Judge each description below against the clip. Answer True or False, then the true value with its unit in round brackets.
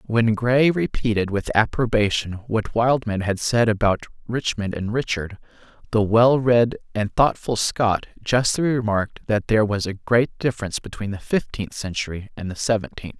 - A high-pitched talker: False (110 Hz)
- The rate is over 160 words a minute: False (155 wpm)